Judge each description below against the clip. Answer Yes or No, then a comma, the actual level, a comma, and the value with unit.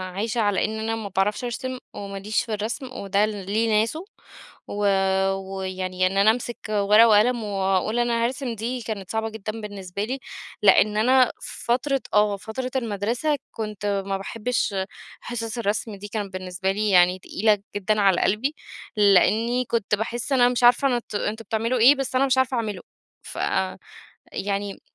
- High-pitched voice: Yes, high, 215 Hz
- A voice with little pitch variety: No, average, 3.2 semitones